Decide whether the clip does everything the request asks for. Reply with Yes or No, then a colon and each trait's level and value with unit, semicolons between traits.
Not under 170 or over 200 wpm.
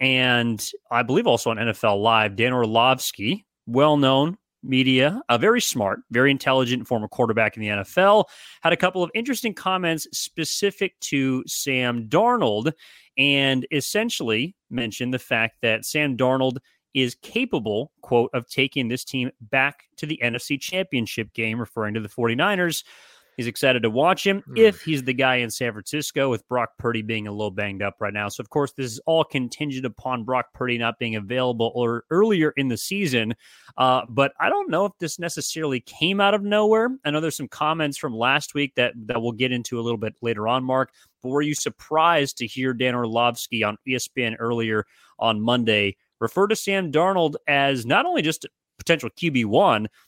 Yes: average, 185 wpm